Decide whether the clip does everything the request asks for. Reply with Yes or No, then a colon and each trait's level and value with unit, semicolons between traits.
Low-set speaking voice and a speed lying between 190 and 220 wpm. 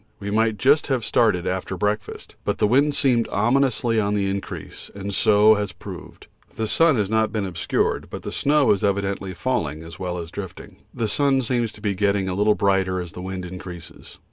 Yes: low, 105 Hz; average, 195 wpm